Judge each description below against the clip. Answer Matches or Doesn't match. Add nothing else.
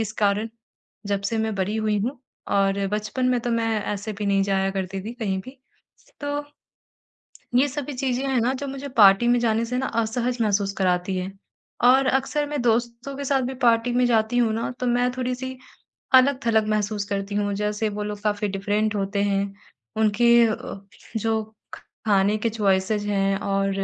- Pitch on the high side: Matches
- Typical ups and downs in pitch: Matches